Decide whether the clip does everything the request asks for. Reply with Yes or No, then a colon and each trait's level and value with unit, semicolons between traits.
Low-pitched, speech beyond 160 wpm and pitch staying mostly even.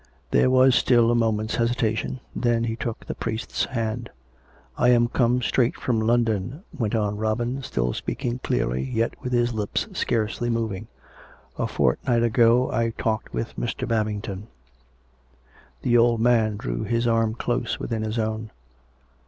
No: low, 115 Hz; average, 155 wpm; narrow, 1.6 semitones